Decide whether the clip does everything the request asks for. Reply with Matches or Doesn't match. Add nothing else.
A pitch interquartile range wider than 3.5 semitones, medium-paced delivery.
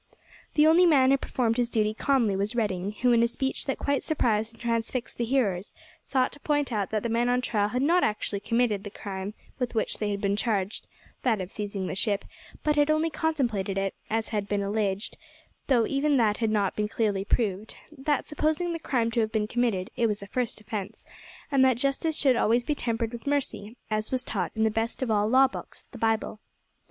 Doesn't match